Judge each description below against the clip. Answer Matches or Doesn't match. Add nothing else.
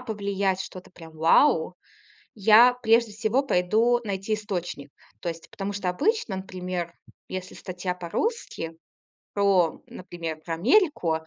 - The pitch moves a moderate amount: Matches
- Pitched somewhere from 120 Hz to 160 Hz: Doesn't match